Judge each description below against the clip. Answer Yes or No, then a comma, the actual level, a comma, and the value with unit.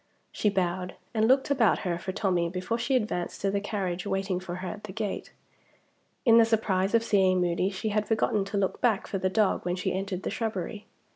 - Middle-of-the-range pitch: No, high, 195 Hz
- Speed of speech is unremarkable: No, fast, 215 wpm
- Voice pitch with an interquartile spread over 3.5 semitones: No, average, 2.8 semitones